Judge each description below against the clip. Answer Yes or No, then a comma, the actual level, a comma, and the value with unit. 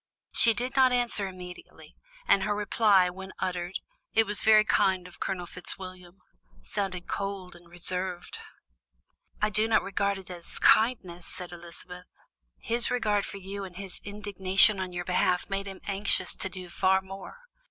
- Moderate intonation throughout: No, narrow, 2.2 semitones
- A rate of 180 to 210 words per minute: No, average, 160 wpm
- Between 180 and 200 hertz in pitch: Yes, high, 190 Hz